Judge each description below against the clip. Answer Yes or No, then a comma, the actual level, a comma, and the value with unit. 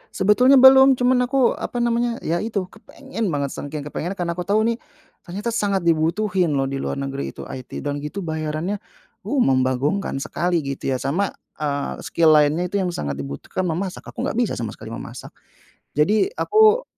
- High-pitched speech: No, medium, 175 Hz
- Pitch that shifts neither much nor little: No, wide, 7.3 semitones